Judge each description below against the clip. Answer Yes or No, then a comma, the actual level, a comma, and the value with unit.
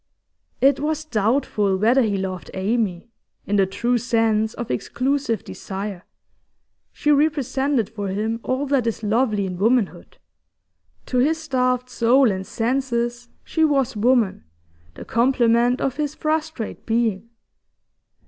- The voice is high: Yes, high, 235 Hz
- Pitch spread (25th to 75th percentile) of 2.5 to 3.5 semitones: No, average, 4.1 semitones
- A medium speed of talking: No, slow, 130 wpm